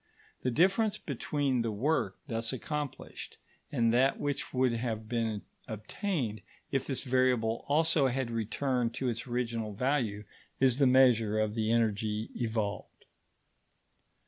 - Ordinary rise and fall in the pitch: Yes, average, 3.3 semitones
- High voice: No, low, 120 Hz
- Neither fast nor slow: No, slow, 130 wpm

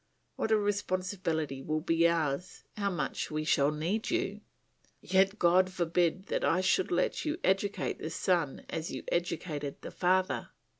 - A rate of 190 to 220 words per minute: No, average, 155 wpm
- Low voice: No, medium, 180 Hz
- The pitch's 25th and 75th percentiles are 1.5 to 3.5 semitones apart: Yes, average, 3.2 semitones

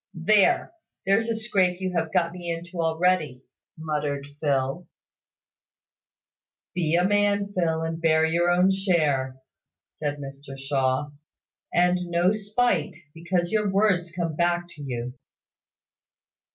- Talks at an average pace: No, slow, 125 wpm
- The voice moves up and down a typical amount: Yes, average, 3.5 semitones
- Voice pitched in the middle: Yes, medium, 170 Hz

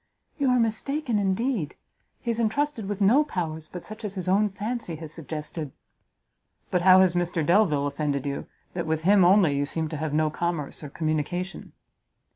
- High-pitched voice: No, medium, 180 Hz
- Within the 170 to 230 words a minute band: Yes, average, 180 wpm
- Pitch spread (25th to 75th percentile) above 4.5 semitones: Yes, average, 5.2 semitones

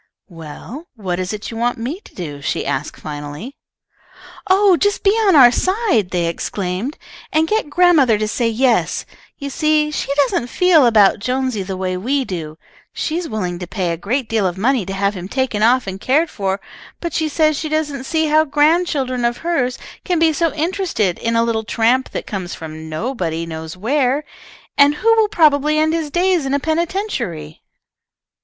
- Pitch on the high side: Yes, very high, 255 Hz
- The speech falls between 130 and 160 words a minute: No, average, 190 wpm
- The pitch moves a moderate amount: No, wide, 8.3 semitones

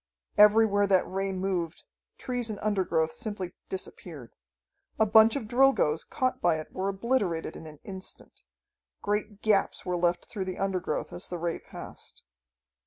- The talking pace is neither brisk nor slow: Yes, average, 150 wpm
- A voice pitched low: No, high, 195 Hz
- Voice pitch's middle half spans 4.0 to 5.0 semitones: No, average, 3.3 semitones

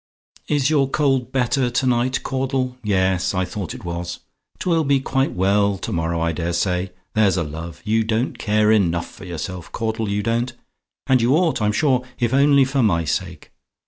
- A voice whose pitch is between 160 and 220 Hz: No, low, 110 Hz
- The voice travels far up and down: Yes, wide, 6.3 semitones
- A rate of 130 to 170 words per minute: No, average, 190 wpm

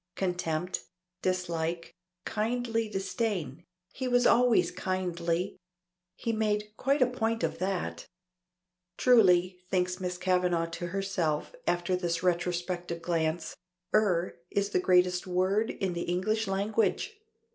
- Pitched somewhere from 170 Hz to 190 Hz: Yes, medium, 185 Hz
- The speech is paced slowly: Yes, slow, 115 wpm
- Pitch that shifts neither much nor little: Yes, average, 3.4 semitones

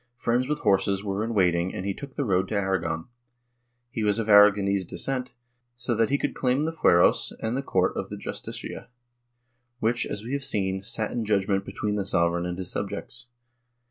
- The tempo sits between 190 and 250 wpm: Yes, average, 195 wpm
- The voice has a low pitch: Yes, low, 105 Hz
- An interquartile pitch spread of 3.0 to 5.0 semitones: Yes, average, 3.8 semitones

